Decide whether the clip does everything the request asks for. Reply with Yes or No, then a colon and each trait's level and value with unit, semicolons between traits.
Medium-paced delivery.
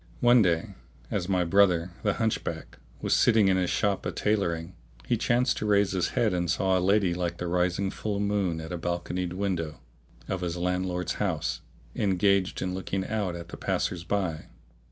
Yes: average, 180 wpm